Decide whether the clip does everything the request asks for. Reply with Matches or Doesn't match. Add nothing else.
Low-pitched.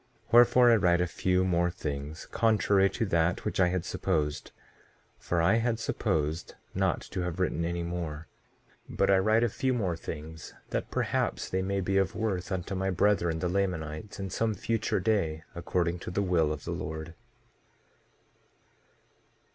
Matches